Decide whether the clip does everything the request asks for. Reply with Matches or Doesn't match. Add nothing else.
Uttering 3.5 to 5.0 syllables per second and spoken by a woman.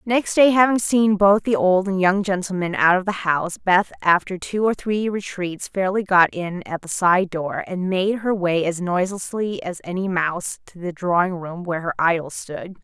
Matches